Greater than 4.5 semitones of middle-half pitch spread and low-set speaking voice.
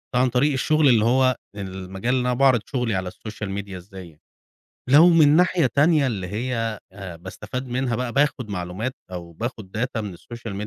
Yes: average, 5.1 semitones; low, 115 Hz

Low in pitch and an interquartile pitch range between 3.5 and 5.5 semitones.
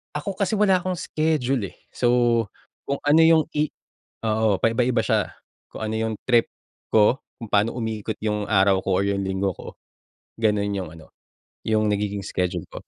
Yes: low, 110 Hz; average, 4.0 semitones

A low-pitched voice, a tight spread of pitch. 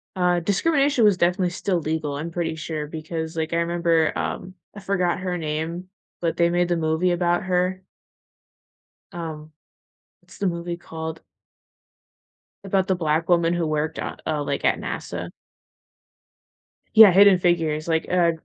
No: medium, 170 Hz; narrow, 2.2 semitones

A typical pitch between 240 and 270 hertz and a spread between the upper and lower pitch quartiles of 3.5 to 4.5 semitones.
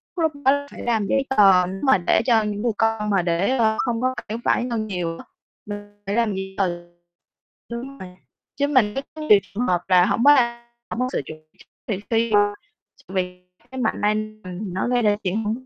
No: high, 215 Hz; average, 4.0 semitones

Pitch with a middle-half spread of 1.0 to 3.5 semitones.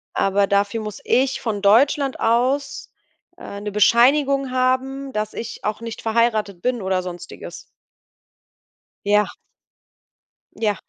No: average, 4.1 semitones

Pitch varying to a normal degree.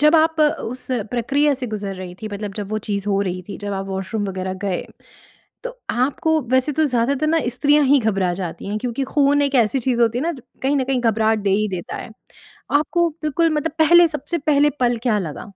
No: wide, 6.2 semitones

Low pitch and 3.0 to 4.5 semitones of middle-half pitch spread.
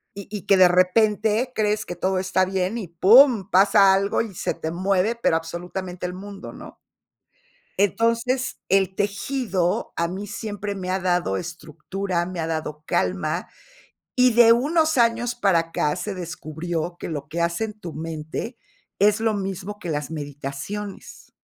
No: high, 190 Hz; average, 3.6 semitones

